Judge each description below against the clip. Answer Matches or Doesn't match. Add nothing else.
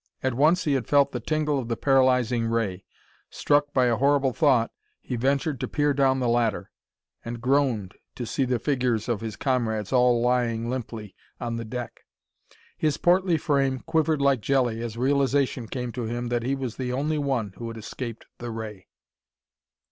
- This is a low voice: Matches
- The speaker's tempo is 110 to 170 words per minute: Doesn't match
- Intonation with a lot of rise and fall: Doesn't match